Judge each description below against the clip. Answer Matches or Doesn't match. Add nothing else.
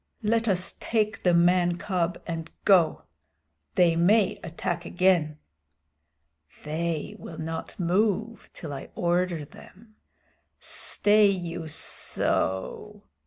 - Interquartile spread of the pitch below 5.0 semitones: Matches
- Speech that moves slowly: Matches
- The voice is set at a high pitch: Doesn't match